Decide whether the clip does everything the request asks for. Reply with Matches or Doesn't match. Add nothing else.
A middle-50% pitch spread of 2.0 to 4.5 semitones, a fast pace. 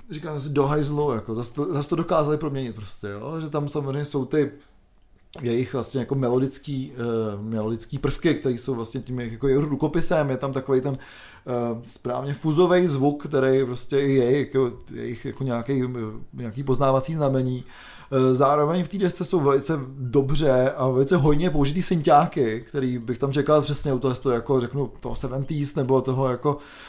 Matches